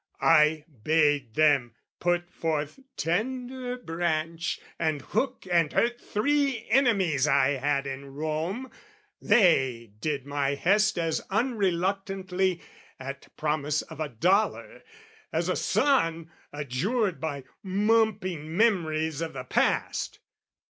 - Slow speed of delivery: Yes, slow, 110 wpm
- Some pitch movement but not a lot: No, wide, 5.7 semitones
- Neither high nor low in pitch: Yes, medium, 165 Hz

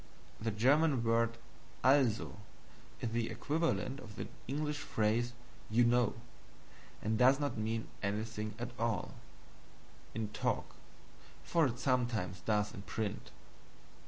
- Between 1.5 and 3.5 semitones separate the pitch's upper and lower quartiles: Yes, average, 3.1 semitones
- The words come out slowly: Yes, slow, 120 wpm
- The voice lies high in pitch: No, low, 115 Hz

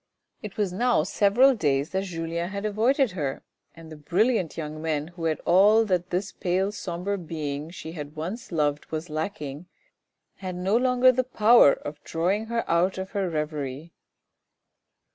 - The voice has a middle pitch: Yes, medium, 180 Hz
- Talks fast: No, average, 160 wpm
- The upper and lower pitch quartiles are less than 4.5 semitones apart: No, average, 4.8 semitones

